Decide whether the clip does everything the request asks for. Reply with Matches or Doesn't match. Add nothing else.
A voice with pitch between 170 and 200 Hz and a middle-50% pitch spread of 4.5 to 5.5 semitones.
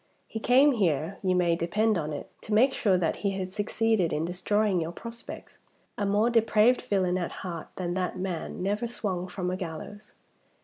Doesn't match